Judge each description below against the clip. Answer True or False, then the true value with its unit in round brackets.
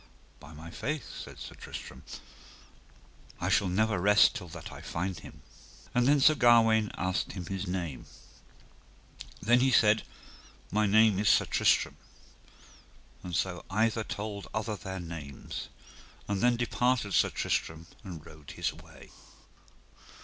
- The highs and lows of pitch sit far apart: False (4.0 semitones)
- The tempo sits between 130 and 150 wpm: True (140 wpm)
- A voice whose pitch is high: False (100 Hz)